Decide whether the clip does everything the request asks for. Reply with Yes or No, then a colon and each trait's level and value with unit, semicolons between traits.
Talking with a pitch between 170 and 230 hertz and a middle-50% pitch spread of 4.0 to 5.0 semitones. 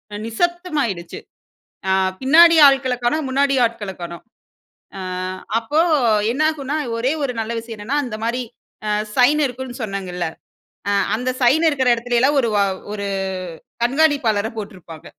No: very high, 250 Hz; average, 4.5 semitones